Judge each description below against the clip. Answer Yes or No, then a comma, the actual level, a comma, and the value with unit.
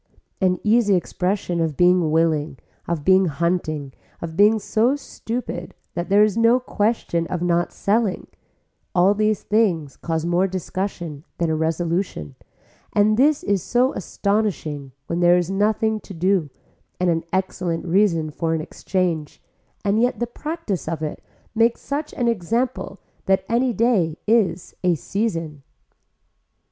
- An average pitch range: Yes, average, 4.5 semitones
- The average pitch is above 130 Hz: Yes, medium, 185 Hz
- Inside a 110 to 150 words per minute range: Yes, average, 145 wpm